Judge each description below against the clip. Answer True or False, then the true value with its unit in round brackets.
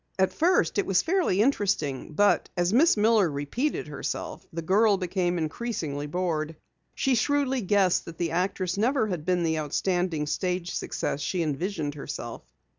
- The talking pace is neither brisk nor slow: True (155 wpm)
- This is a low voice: False (180 Hz)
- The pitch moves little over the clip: False (4.7 semitones)